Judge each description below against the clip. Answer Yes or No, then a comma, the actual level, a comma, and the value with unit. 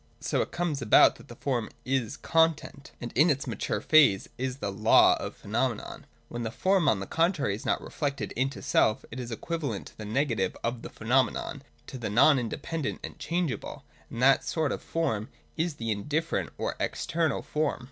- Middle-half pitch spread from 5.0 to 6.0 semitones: Yes, wide, 5.4 semitones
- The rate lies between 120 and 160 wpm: No, average, 195 wpm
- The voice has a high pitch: No, low, 135 Hz